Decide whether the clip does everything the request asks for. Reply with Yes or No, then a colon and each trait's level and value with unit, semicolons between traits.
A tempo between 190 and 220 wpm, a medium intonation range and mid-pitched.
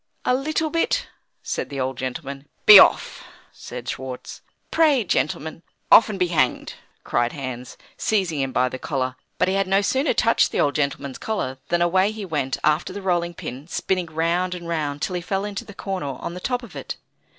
No: average, 200 wpm; wide, 6.0 semitones; medium, 170 Hz